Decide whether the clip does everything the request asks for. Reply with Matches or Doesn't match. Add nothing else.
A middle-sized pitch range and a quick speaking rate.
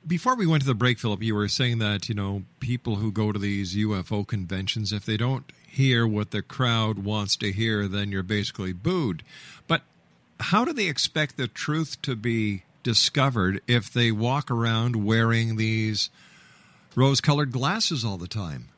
Doesn't match